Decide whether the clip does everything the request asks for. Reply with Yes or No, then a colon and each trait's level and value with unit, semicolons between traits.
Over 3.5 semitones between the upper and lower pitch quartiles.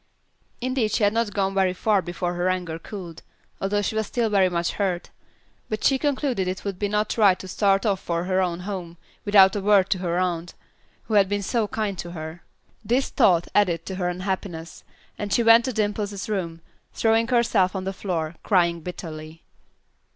No: average, 3.0 semitones